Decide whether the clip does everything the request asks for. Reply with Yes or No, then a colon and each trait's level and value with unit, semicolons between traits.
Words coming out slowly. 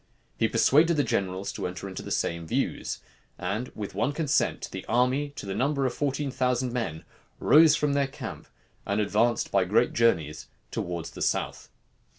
No: average, 170 wpm